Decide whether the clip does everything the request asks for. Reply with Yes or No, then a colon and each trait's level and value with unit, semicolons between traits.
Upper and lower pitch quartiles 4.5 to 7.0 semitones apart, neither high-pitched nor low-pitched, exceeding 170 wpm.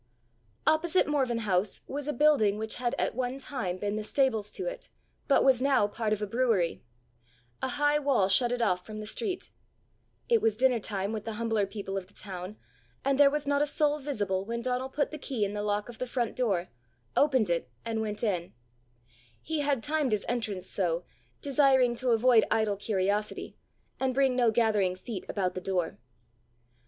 No: average, 4.8 semitones; high, 230 Hz; average, 190 wpm